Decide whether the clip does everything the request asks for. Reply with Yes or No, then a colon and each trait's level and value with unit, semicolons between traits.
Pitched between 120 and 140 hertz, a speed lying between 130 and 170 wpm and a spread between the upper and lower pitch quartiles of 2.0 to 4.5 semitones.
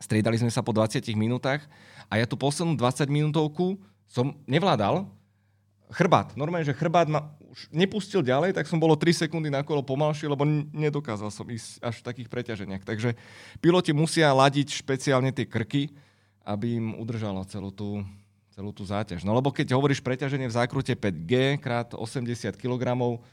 No: low, 125 Hz; fast, 165 wpm; average, 5.1 semitones